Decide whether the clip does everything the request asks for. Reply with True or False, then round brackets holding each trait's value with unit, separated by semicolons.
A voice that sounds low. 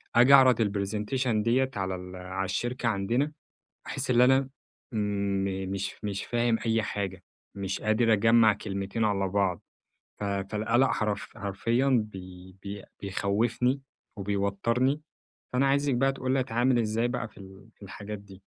True (105 Hz)